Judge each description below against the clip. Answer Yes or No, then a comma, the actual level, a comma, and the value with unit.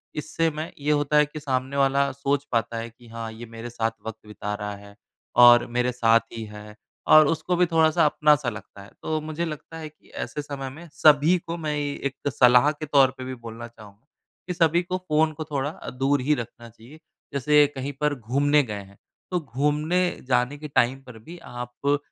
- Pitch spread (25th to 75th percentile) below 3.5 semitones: No, average, 4.2 semitones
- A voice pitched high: No, medium, 140 Hz